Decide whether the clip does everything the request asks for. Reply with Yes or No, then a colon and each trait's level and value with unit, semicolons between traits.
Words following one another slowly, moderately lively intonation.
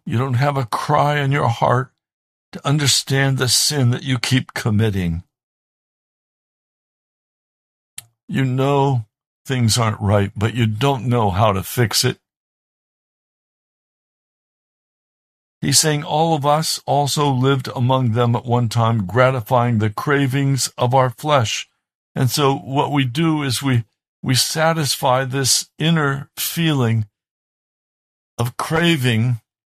Yes: slow, 125 wpm; average, 3.3 semitones